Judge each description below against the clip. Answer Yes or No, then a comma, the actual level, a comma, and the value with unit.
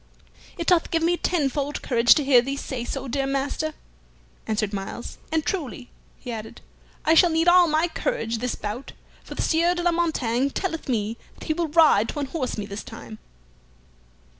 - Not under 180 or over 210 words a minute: Yes, average, 185 wpm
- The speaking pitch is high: Yes, very high, 280 Hz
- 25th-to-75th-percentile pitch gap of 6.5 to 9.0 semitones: No, wide, 5.6 semitones